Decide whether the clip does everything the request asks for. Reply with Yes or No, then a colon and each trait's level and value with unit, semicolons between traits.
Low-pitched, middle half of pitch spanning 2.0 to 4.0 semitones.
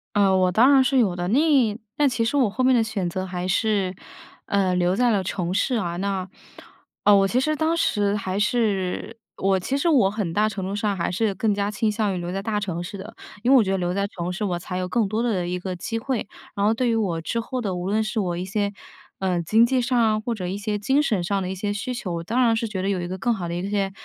No: high, 205 Hz; average, 3.6 semitones